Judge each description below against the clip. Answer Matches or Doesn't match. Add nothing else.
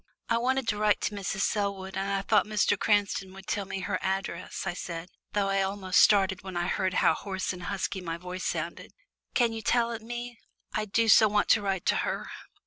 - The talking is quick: Matches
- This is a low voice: Doesn't match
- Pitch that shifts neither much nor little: Doesn't match